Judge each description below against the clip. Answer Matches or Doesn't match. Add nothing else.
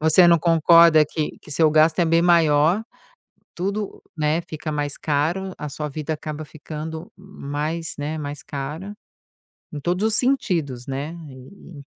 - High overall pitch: Doesn't match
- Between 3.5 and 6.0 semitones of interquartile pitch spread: Doesn't match